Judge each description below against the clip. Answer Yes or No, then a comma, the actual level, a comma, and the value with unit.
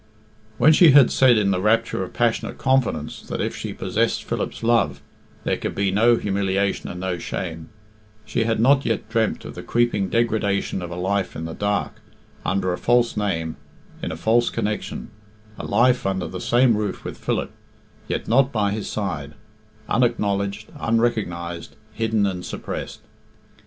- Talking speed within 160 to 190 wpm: Yes, average, 165 wpm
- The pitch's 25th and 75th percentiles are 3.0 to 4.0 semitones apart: Yes, average, 3.7 semitones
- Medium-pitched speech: No, low, 105 Hz